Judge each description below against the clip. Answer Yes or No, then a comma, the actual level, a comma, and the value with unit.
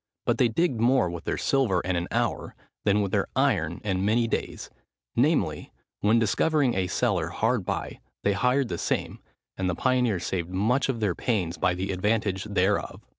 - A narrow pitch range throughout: No, average, 4.7 semitones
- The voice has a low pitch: Yes, low, 105 Hz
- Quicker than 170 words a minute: Yes, average, 180 wpm